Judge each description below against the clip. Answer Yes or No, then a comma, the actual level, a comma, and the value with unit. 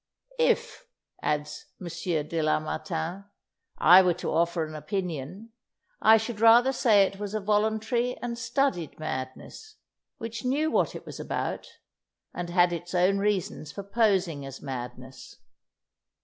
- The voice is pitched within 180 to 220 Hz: Yes, high, 190 Hz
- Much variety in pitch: Yes, wide, 5.9 semitones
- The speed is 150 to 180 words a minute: No, slow, 135 wpm